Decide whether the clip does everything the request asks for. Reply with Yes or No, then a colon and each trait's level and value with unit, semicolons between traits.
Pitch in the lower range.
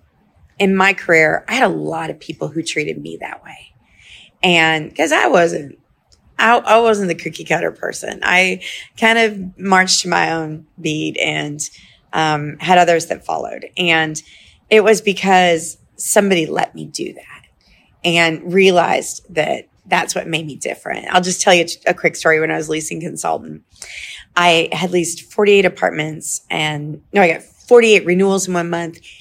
No: medium, 170 Hz